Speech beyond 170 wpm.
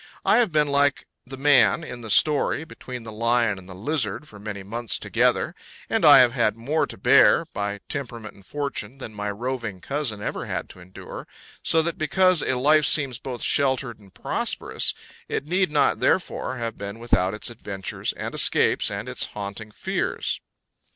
Yes: average, 180 wpm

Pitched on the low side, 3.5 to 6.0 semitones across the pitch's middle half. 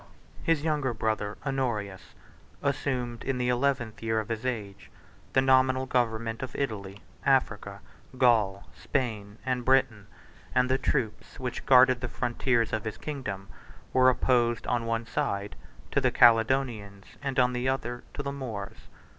No: low, 120 Hz; average, 3.1 semitones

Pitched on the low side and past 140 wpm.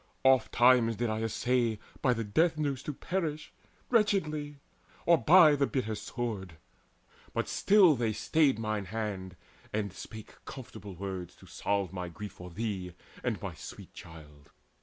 Yes: low, 115 Hz; average, 150 wpm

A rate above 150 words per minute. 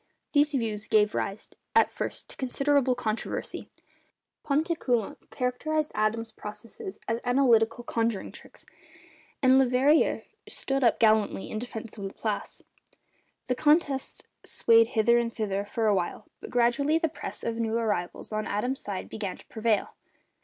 No: average, 140 wpm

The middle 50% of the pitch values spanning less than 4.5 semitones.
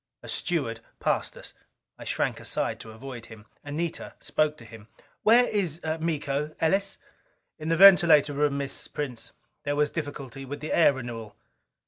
Yes: average, 3.9 semitones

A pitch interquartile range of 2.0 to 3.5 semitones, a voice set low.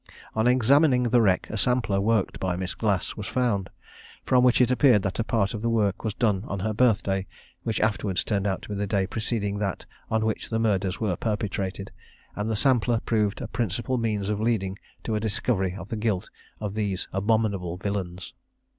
Yes: average, 2.7 semitones; low, 105 Hz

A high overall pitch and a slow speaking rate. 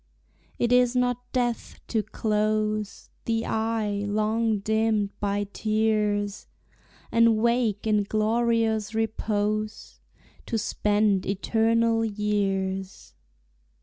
Yes: high, 215 Hz; slow, 90 wpm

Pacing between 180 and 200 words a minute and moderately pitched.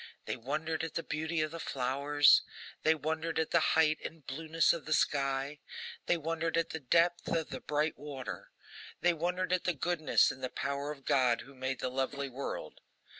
Yes: average, 190 wpm; medium, 155 Hz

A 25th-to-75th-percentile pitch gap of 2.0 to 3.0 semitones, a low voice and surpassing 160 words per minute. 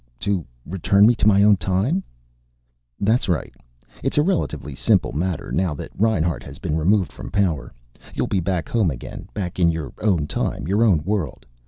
No: average, 4.2 semitones; very low, 95 Hz; average, 180 wpm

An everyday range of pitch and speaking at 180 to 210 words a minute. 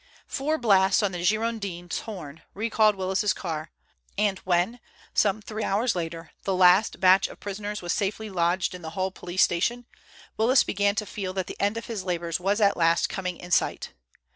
Yes: average, 3.1 semitones; average, 185 wpm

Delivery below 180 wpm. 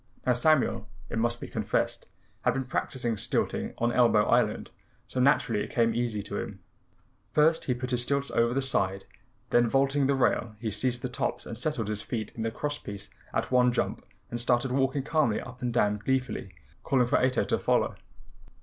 No: average, 195 wpm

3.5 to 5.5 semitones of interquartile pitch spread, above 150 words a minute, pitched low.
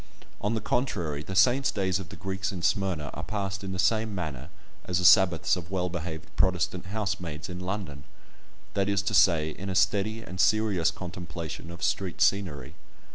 No: average, 2.7 semitones; average, 180 wpm; very low, 95 Hz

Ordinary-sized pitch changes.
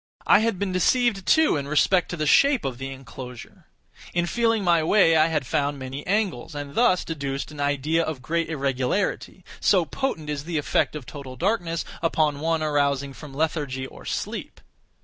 Yes: average, 4.3 semitones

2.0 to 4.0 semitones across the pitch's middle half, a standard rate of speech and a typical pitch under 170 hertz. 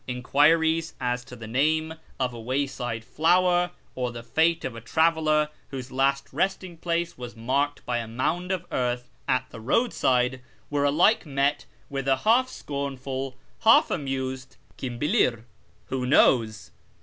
No: average, 4.4 semitones; average, 160 wpm; low, 135 Hz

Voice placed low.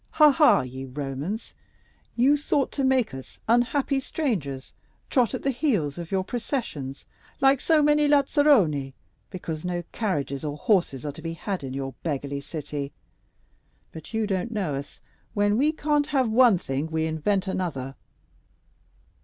No: medium, 185 Hz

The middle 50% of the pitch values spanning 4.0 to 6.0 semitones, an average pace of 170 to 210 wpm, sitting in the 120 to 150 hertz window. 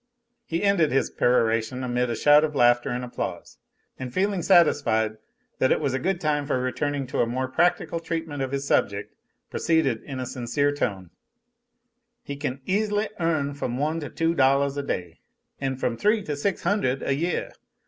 Yes: average, 4.5 semitones; average, 180 wpm; medium, 140 Hz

